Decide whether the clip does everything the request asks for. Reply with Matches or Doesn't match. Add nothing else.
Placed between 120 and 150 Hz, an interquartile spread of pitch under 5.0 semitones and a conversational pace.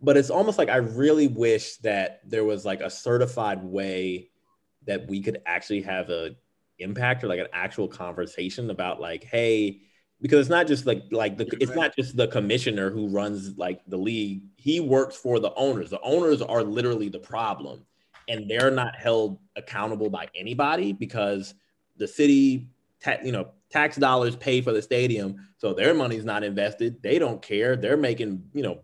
Doesn't match